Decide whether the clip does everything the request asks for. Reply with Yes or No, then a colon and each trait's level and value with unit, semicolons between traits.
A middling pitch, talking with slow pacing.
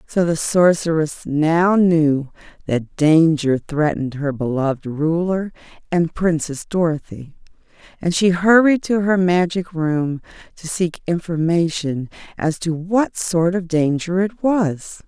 Yes: medium, 165 Hz; slow, 125 wpm